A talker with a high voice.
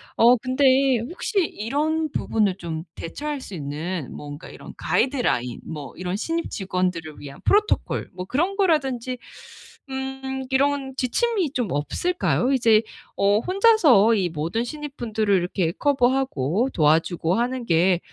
Yes: high, 240 Hz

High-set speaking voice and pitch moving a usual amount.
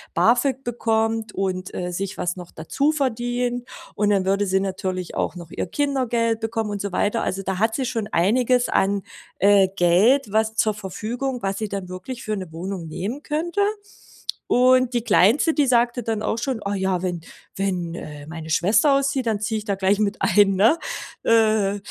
Yes: high, 210 Hz; average, 4.1 semitones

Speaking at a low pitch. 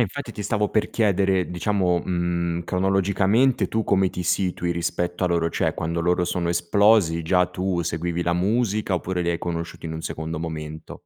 Yes: very low, 90 Hz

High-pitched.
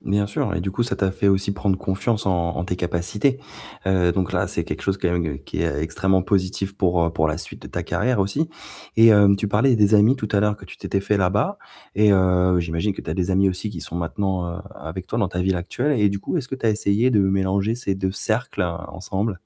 No: very low, 95 Hz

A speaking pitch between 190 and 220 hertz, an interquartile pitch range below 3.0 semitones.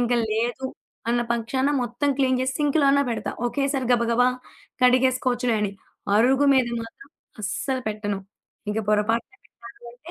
No: high, 245 Hz; narrow, 2.4 semitones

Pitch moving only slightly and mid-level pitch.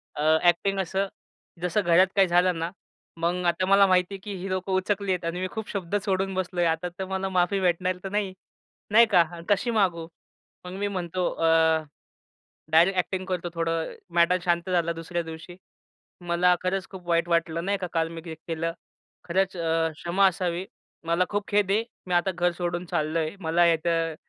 Yes: narrow, 2.1 semitones; medium, 180 Hz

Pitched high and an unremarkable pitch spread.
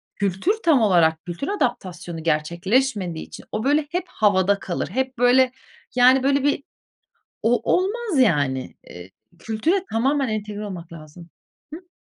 No: high, 215 Hz; wide, 7.6 semitones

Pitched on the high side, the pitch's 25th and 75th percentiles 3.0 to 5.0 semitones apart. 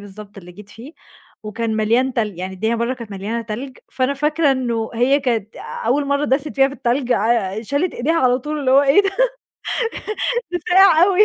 Yes: very high, 250 Hz; average, 4.4 semitones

